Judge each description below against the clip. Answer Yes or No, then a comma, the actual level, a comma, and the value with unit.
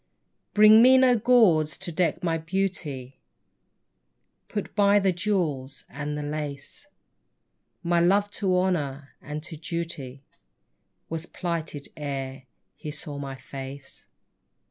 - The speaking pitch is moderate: Yes, medium, 165 Hz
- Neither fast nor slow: No, slow, 120 wpm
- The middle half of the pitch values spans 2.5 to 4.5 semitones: No, average, 5.0 semitones